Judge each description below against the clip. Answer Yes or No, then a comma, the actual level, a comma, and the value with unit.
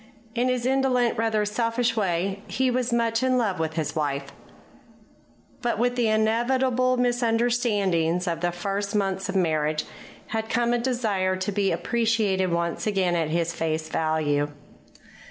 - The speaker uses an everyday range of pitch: No, wide, 5.7 semitones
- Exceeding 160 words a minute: No, average, 150 wpm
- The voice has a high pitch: Yes, high, 210 Hz